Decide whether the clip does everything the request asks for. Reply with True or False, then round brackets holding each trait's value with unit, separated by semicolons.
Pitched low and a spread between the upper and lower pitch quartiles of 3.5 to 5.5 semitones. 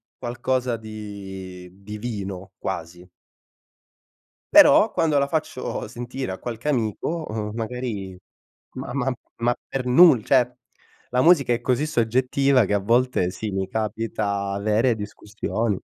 True (115 Hz; 3.9 semitones)